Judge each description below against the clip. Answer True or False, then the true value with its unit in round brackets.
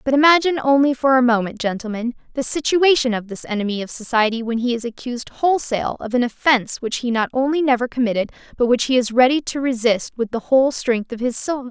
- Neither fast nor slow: False (215 wpm)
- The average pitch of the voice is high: True (250 Hz)